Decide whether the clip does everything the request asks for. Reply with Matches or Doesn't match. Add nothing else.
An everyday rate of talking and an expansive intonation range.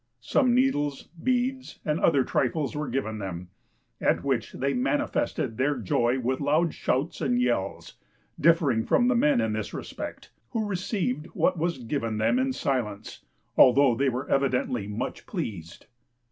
Matches